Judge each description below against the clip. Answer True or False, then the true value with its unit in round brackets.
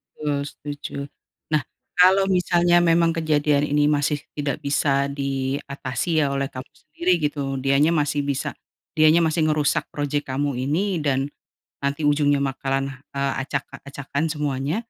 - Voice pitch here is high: False (145 Hz)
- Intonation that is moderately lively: False (2.0 semitones)